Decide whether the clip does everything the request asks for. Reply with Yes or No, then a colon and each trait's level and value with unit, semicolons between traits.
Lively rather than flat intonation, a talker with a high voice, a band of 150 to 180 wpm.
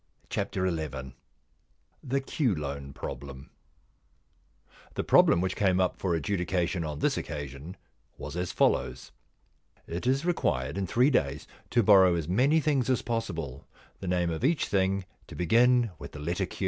No: wide, 7.2 semitones; very low, 90 Hz; average, 160 wpm